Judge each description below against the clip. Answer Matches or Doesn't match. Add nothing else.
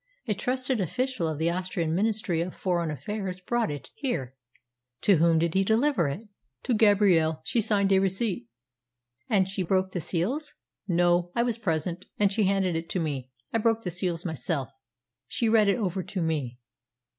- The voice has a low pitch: Doesn't match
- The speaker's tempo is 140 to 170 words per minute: Doesn't match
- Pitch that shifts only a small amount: Doesn't match